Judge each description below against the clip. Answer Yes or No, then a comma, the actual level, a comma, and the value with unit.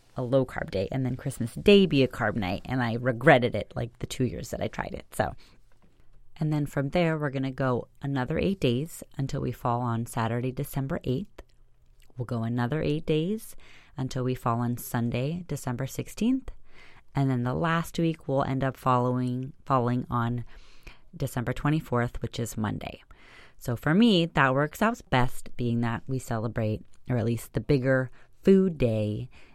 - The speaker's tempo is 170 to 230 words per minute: Yes, average, 180 wpm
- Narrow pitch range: No, average, 3.3 semitones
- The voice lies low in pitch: Yes, low, 130 Hz